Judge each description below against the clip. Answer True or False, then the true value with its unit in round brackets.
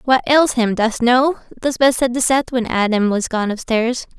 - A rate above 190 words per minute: True (200 wpm)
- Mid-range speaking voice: False (245 Hz)